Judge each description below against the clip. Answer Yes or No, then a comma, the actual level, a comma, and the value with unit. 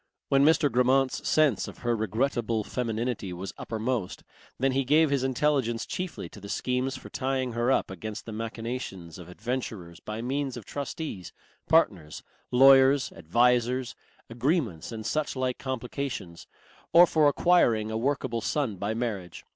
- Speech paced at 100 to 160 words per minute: Yes, average, 140 wpm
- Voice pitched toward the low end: Yes, low, 125 Hz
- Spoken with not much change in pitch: No, average, 3.7 semitones